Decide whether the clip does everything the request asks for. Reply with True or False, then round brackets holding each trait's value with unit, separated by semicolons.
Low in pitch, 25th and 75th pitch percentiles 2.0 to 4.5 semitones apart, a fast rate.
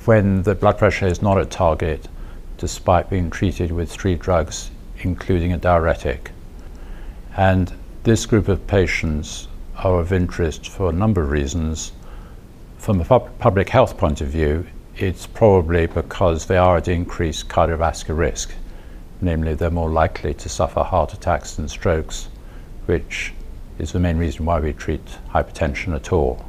False (85 Hz; 2.9 semitones; 155 wpm)